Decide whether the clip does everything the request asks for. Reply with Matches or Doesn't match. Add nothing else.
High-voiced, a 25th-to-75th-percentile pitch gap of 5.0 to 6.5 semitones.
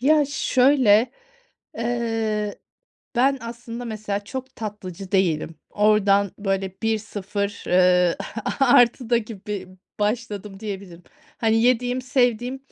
Doesn't match